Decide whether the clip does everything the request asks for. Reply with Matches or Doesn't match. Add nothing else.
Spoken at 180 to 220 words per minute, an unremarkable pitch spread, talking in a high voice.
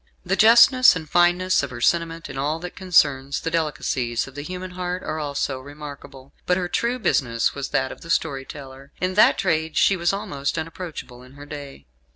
Doesn't match